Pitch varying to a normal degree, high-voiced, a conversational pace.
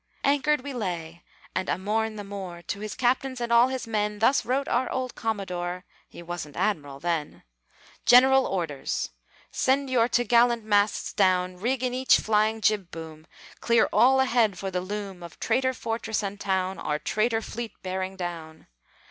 Yes: average, 5.0 semitones; high, 210 Hz; average, 165 wpm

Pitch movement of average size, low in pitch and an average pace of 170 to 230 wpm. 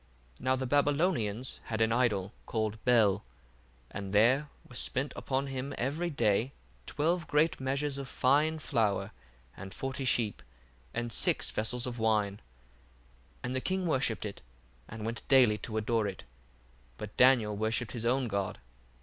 No: average, 3.9 semitones; low, 120 Hz; average, 155 wpm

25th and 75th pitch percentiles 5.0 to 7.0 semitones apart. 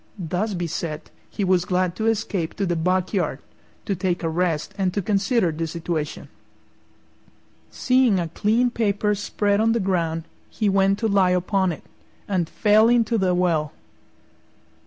No: average, 3.3 semitones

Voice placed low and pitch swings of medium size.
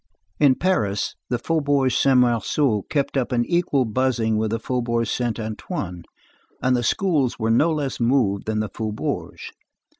Yes: low, 120 Hz; average, 3.9 semitones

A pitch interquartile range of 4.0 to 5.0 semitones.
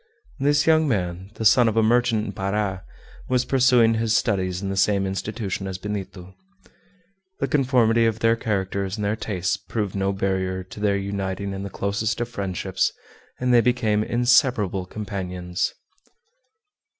No: average, 3.2 semitones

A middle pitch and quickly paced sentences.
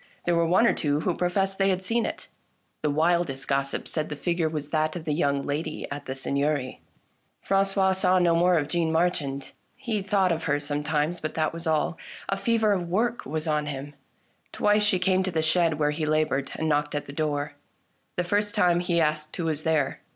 Yes: medium, 160 Hz; fast, 215 wpm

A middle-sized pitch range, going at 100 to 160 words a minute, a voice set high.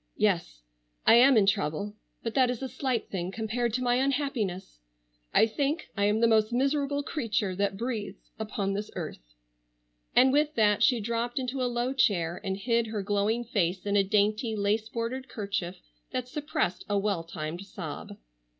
No: average, 3.9 semitones; average, 175 wpm; high, 220 Hz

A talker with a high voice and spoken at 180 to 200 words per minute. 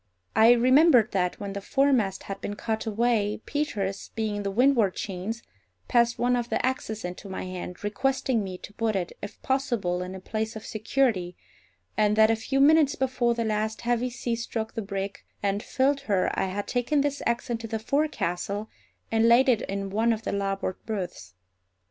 Yes: high, 220 Hz; average, 190 wpm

